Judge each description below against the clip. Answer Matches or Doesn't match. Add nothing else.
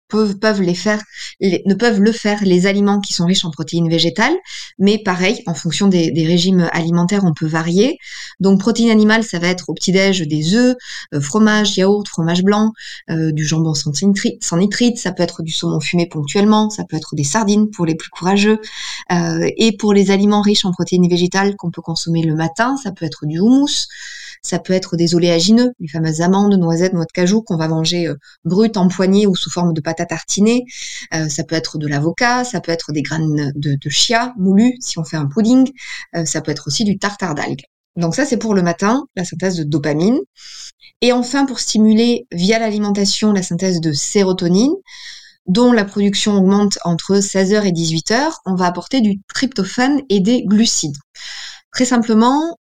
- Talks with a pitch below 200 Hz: Matches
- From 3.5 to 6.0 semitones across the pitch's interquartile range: Matches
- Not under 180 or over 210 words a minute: Matches